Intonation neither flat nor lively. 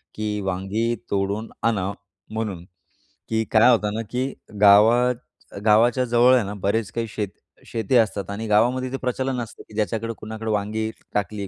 No: narrow, 2.3 semitones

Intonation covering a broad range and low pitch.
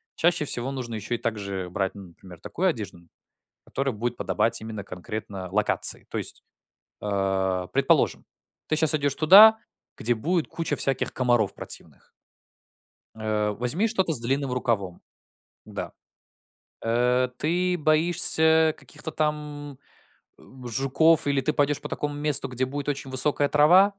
Yes: wide, 6.1 semitones; low, 130 Hz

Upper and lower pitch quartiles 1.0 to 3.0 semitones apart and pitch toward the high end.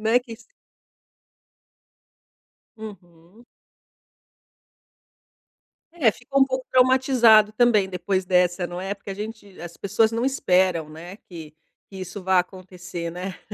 No: average, 4.1 semitones; high, 195 Hz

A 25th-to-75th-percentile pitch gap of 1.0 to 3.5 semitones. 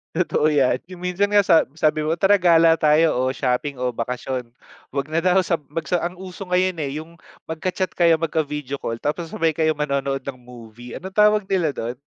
No: average, 4.5 semitones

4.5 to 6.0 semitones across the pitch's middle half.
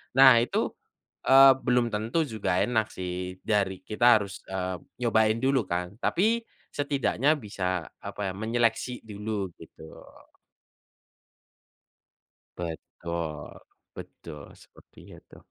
Yes: average, 5.1 semitones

